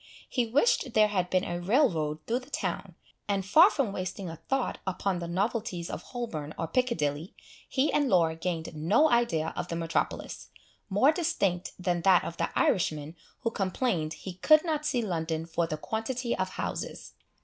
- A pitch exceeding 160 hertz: Yes, high, 190 Hz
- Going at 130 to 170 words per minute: No, average, 180 wpm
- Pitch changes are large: Yes, wide, 6.4 semitones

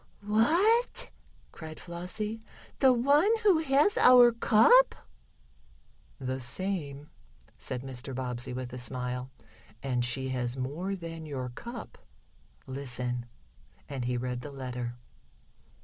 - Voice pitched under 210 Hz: Yes, medium, 140 Hz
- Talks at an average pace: No, slow, 115 wpm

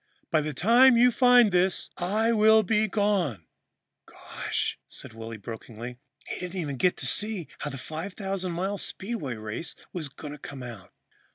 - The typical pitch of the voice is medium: Yes, medium, 180 Hz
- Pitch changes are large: Yes, wide, 7.8 semitones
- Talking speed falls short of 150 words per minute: No, average, 165 wpm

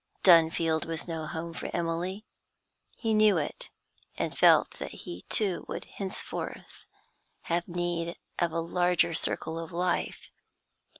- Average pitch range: No, narrow, 1.5 semitones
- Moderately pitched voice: Yes, medium, 170 Hz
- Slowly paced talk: Yes, slow, 130 wpm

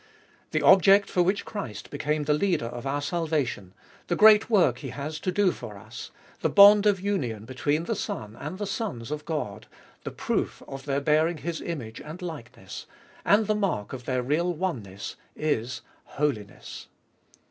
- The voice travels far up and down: Yes, wide, 7.1 semitones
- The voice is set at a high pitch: No, medium, 150 Hz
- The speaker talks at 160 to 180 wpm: Yes, average, 170 wpm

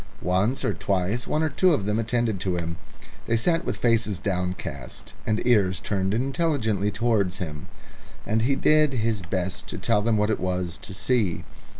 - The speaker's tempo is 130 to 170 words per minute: No, average, 180 wpm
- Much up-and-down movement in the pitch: No, average, 4.3 semitones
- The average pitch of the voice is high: No, low, 105 Hz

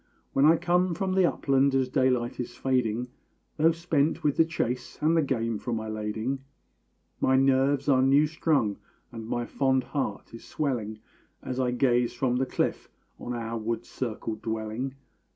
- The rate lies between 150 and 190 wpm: Yes, average, 170 wpm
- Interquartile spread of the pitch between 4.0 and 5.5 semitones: No, average, 3.4 semitones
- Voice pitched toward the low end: Yes, low, 130 Hz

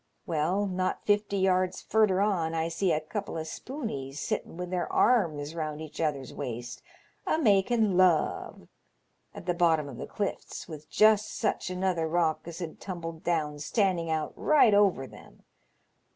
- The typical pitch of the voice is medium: Yes, medium, 175 Hz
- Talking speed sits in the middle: Yes, average, 160 wpm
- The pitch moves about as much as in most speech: Yes, average, 4.0 semitones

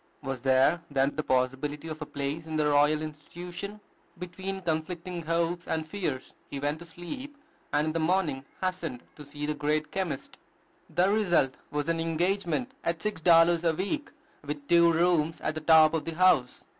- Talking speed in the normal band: Yes, average, 180 wpm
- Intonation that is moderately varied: Yes, average, 3.0 semitones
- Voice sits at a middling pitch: Yes, medium, 160 Hz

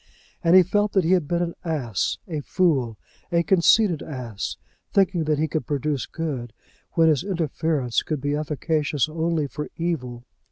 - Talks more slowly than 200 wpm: Yes, average, 165 wpm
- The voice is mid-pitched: Yes, medium, 155 Hz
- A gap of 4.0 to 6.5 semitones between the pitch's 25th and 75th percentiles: No, average, 3.2 semitones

